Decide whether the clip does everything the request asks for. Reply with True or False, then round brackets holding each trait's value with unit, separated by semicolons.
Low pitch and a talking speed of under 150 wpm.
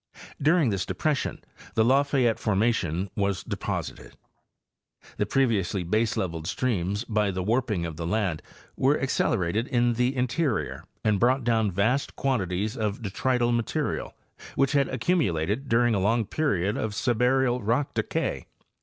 True (115 Hz; 140 wpm)